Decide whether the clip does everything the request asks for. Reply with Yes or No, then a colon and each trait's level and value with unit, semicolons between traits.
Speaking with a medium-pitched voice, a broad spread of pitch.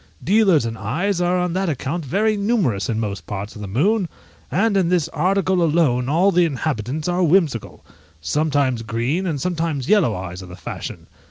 Yes: medium, 160 Hz; wide, 7.5 semitones